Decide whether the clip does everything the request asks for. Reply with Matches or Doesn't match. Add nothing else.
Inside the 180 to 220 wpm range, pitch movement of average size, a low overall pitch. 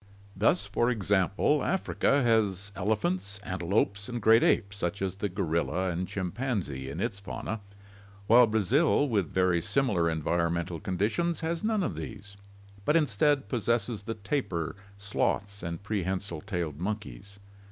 Doesn't match